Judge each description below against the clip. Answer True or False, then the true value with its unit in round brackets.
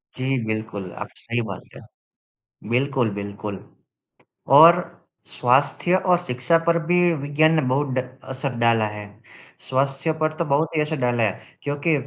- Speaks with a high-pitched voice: False (135 Hz)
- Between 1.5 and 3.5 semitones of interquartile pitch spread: False (4.9 semitones)